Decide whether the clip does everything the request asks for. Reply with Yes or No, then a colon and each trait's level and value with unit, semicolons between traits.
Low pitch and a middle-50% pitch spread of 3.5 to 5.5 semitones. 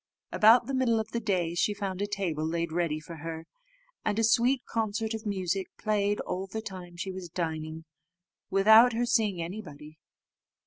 No: high, 195 Hz; average, 4.5 semitones